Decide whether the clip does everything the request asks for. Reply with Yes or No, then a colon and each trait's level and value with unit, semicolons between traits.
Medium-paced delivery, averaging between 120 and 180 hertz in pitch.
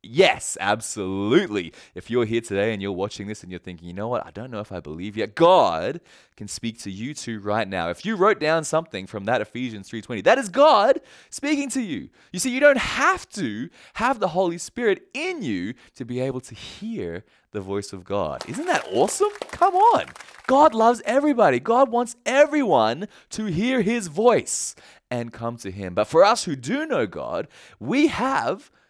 Yes: average, 195 wpm; low, 135 Hz